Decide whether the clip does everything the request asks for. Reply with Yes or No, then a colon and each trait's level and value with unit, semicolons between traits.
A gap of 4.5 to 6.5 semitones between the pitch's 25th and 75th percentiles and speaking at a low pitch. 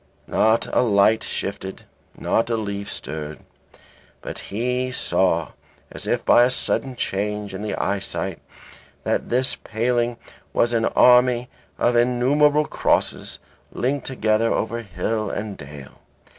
No: average, 3.5 semitones; low, 115 Hz